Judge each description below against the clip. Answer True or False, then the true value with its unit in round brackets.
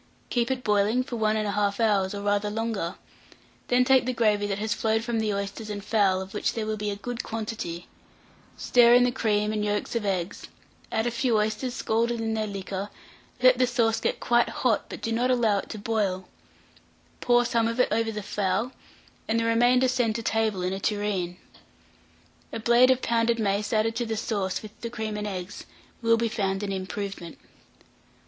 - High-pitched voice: True (220 Hz)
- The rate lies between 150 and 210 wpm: True (200 wpm)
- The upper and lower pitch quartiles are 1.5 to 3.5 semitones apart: True (2.4 semitones)